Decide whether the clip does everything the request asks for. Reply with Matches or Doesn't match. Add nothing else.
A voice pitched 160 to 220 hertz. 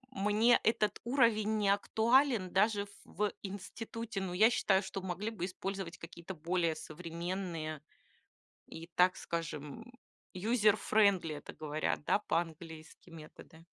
Matches